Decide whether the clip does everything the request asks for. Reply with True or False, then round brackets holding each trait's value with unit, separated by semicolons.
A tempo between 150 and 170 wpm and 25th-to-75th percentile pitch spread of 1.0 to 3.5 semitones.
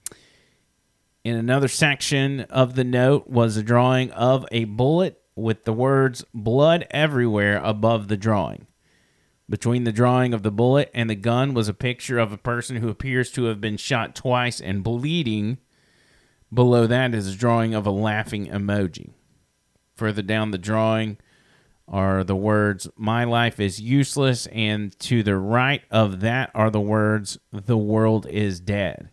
True (160 wpm; 2.9 semitones)